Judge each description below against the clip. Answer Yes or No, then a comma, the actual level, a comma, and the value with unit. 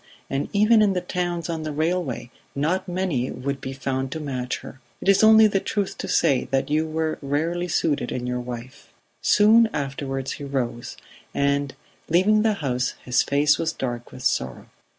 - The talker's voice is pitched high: No, medium, 145 Hz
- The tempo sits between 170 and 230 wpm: Yes, average, 180 wpm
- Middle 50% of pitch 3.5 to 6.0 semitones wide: Yes, average, 5.2 semitones